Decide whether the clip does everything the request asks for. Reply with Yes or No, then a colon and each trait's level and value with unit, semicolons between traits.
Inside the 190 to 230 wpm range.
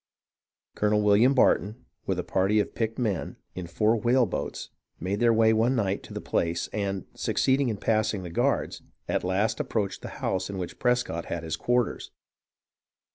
No: average, 175 wpm